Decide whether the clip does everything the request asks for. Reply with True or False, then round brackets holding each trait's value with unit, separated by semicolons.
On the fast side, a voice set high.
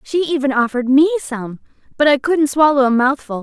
False (195 wpm; 275 Hz)